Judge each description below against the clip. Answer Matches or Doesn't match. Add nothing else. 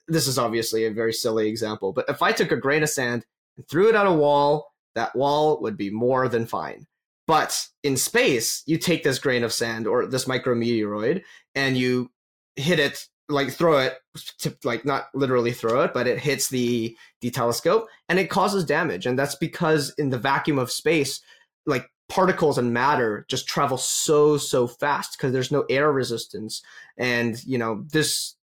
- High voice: Doesn't match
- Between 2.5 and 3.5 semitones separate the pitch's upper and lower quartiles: Doesn't match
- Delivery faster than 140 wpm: Matches